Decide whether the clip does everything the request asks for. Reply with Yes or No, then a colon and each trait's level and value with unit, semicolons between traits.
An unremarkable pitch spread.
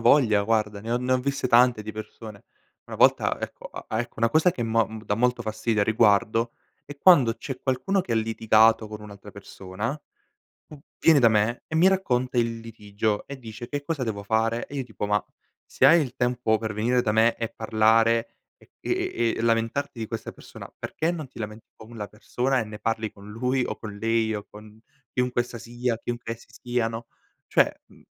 No: narrow, 2.3 semitones